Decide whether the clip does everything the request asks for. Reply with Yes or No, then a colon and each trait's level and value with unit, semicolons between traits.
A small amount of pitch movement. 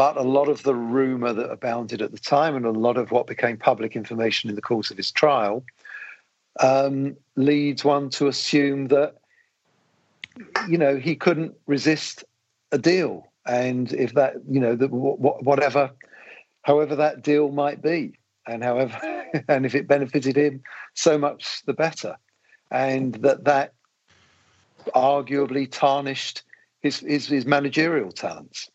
Yes: narrow, 2.1 semitones